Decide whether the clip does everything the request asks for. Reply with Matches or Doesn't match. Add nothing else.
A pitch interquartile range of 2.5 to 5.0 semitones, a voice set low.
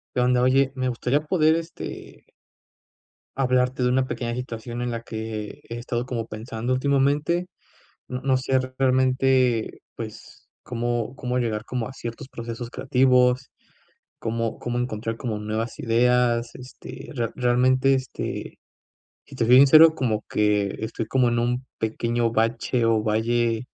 Doesn't match